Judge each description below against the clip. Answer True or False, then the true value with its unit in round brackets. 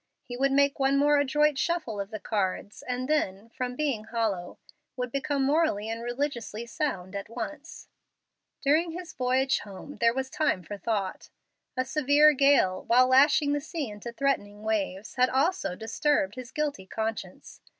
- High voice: True (255 Hz)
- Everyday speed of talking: True (160 wpm)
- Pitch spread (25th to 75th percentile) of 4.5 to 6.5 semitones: True (5.0 semitones)